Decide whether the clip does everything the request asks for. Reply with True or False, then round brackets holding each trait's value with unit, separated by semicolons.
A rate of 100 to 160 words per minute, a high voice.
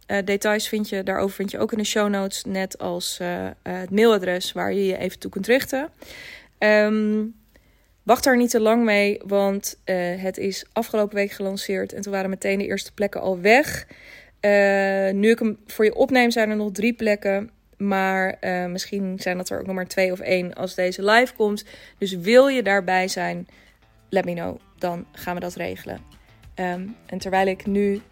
False (200 wpm; 195 Hz)